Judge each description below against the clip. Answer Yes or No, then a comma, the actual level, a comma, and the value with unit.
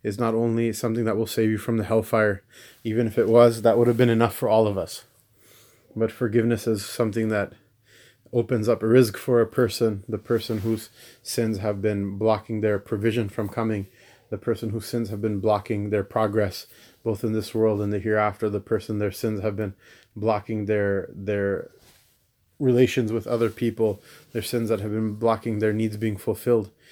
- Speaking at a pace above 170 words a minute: Yes, average, 190 wpm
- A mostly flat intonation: Yes, narrow, 1.5 semitones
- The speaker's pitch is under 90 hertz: No, low, 110 Hz